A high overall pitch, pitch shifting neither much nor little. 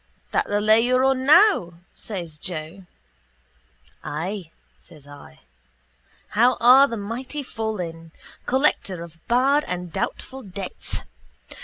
No: high, 205 Hz; wide, 7.0 semitones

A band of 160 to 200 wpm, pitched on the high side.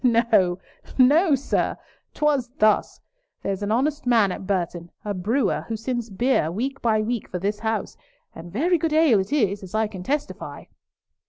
Yes: average, 170 wpm; high, 225 Hz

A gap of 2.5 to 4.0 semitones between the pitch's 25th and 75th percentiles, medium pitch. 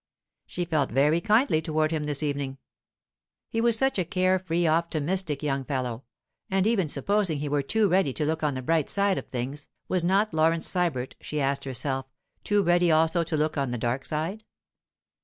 No: average, 4.6 semitones; medium, 160 Hz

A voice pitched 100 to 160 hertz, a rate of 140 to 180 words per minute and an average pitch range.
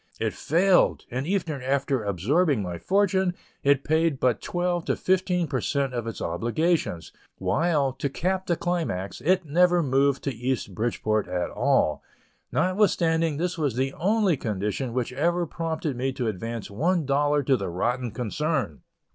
No: medium, 140 Hz; average, 160 wpm; wide, 6.3 semitones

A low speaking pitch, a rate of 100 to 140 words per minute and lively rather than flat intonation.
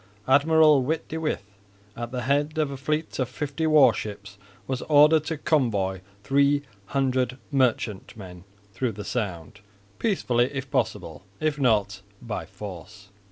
Yes: low, 130 Hz; slow, 135 wpm; wide, 5.7 semitones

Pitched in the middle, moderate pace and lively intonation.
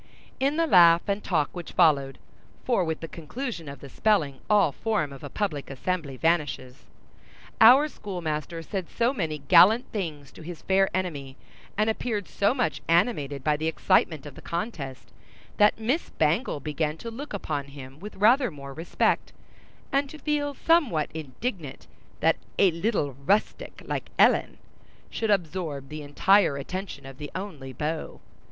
Yes: medium, 170 Hz; average, 160 wpm; wide, 6.3 semitones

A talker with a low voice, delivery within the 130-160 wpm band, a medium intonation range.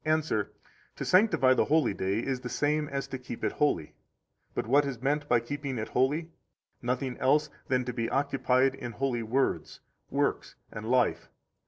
No: low, 130 Hz; average, 175 wpm; average, 3.1 semitones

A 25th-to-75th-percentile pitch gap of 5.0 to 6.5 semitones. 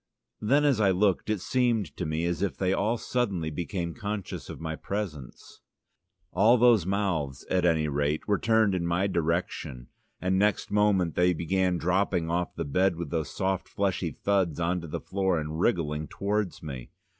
No: average, 3.6 semitones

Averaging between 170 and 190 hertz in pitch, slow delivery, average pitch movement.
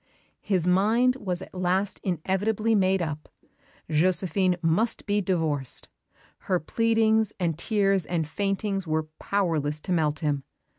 Yes: medium, 185 Hz; slow, 130 wpm; average, 3.9 semitones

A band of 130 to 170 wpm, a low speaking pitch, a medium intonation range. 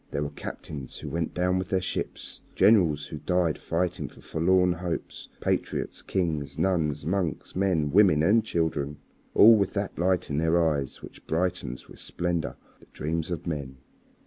Yes: average, 165 wpm; very low, 85 Hz; average, 3.3 semitones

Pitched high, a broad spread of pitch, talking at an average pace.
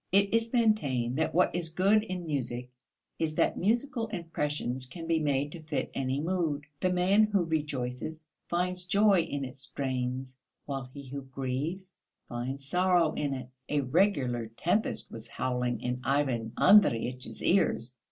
No: medium, 150 Hz; wide, 5.9 semitones; average, 150 wpm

